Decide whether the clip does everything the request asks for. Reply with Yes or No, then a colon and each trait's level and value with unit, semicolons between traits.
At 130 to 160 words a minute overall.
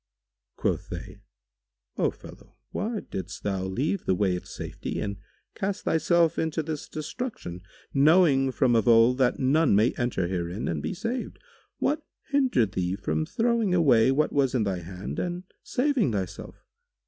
Yes: average, 155 wpm